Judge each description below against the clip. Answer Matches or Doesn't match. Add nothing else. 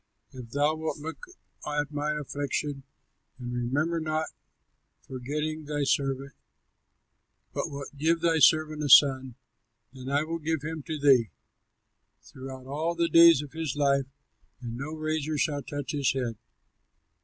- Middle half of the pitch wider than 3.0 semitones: Doesn't match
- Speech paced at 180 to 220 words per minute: Doesn't match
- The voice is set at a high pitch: Doesn't match